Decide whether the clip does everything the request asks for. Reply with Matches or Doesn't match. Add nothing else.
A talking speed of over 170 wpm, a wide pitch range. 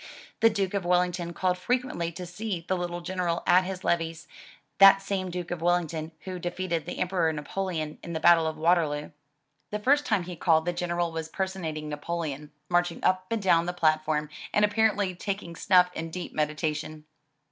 Doesn't match